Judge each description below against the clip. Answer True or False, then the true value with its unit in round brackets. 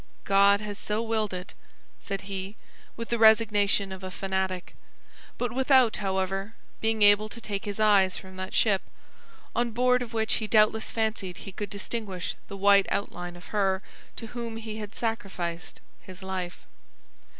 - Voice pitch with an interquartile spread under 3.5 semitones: True (2.6 semitones)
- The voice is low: False (205 Hz)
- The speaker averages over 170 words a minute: False (160 wpm)